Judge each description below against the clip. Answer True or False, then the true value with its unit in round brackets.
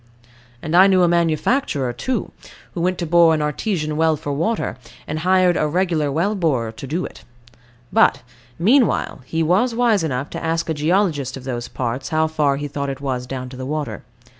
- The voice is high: False (160 Hz)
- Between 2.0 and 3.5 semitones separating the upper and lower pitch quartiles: False (4.3 semitones)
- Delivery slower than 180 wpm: False (195 wpm)